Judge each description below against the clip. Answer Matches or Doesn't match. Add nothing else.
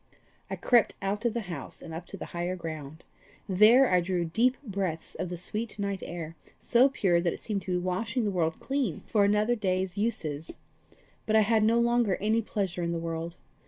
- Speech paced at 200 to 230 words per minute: Matches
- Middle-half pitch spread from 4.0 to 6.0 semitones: Matches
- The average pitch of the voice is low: Doesn't match